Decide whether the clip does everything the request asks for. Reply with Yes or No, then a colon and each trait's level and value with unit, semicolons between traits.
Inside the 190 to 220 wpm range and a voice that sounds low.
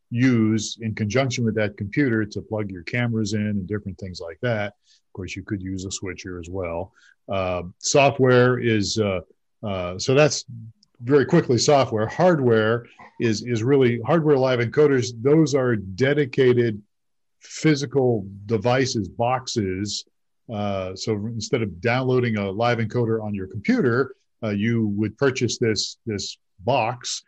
No: average, 145 wpm; low, 115 Hz